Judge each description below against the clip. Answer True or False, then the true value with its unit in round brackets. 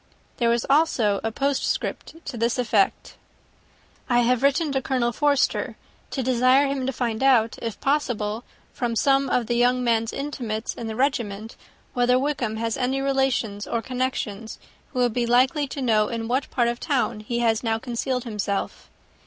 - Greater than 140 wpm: True (175 wpm)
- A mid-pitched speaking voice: False (245 Hz)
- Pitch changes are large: False (2.8 semitones)